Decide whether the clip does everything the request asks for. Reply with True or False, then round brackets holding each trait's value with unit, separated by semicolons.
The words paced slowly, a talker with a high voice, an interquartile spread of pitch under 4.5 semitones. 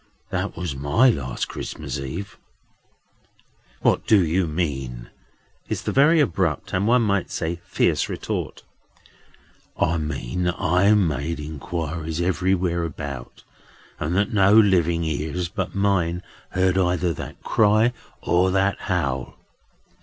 False (125 wpm; 90 Hz; 3.7 semitones)